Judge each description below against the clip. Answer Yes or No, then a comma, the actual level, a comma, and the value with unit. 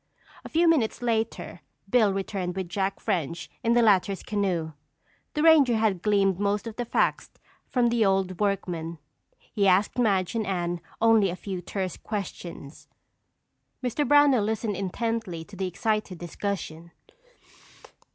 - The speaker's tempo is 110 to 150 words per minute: Yes, average, 140 wpm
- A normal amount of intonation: Yes, average, 3.7 semitones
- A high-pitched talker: Yes, high, 200 Hz